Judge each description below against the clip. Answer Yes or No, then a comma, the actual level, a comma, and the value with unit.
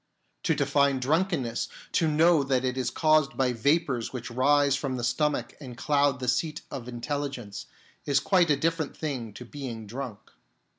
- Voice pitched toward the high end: No, low, 135 Hz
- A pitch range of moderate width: Yes, average, 3.3 semitones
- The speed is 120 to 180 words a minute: No, average, 190 wpm